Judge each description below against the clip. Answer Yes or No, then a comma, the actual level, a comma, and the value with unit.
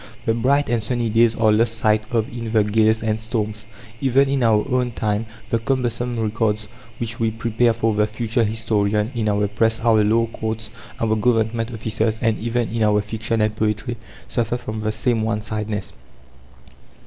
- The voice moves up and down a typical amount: No, narrow, 1.4 semitones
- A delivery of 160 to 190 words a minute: Yes, average, 180 wpm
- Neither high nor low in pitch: No, low, 110 Hz